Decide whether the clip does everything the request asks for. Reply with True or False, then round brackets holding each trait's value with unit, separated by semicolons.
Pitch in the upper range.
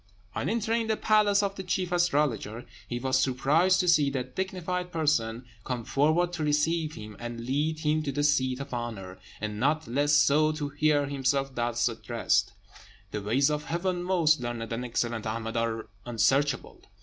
False (145 Hz)